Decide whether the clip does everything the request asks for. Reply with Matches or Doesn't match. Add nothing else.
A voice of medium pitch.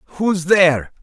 Matches